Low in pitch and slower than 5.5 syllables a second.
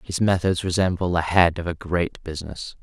Yes: very low, 85 Hz; 5.2 syllables/s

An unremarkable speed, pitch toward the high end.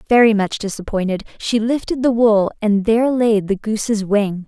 Yes: average, 175 wpm; high, 215 Hz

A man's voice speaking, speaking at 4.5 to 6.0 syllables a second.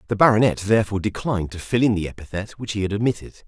No: male; 7.6 syllables/s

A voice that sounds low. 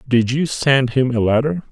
Yes: low, 130 Hz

